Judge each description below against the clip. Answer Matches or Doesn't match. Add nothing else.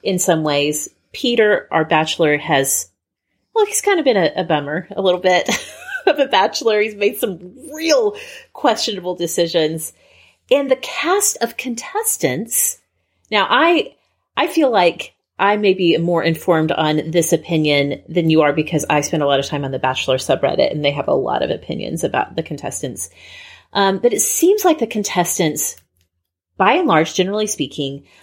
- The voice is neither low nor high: Matches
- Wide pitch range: Matches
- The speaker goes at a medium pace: Matches